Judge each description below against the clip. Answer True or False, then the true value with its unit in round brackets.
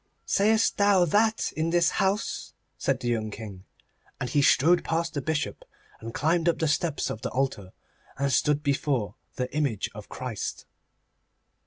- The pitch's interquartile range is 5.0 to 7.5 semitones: True (5.4 semitones)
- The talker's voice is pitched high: False (150 Hz)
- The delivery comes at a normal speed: True (160 wpm)